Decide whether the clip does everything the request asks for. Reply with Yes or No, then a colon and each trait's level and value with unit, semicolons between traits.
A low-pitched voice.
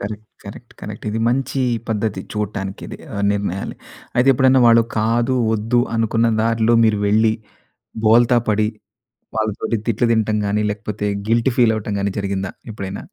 Yes: low, 110 Hz